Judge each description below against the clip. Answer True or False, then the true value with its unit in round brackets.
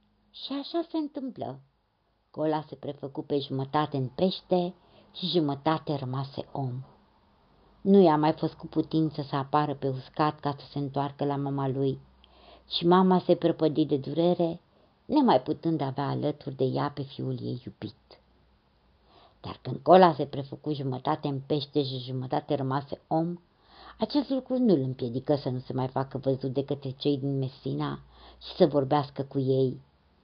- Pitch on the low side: False (145 Hz)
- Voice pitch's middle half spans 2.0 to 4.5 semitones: True (3.1 semitones)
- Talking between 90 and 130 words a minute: False (160 wpm)